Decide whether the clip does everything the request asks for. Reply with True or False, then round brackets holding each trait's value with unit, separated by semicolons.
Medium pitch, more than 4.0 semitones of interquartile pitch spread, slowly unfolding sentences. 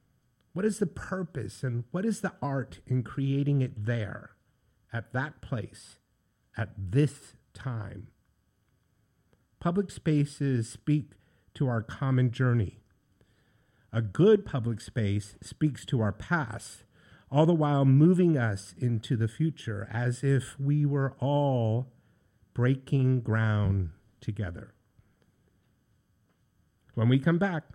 False (125 Hz; 4.4 semitones; 115 wpm)